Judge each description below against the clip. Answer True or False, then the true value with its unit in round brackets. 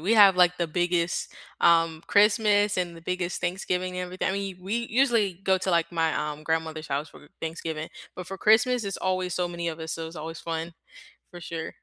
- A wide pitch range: False (2.9 semitones)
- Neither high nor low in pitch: True (175 Hz)